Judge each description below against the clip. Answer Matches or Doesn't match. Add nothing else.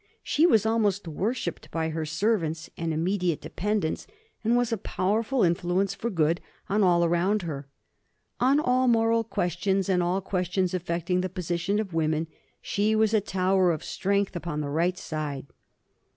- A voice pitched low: Doesn't match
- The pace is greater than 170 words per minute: Doesn't match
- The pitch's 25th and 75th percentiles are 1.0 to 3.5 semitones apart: Doesn't match